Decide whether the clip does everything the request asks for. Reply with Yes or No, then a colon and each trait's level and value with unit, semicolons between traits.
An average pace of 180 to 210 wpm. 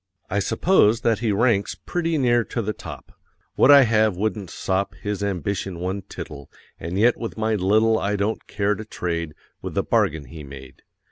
Yes: average, 185 wpm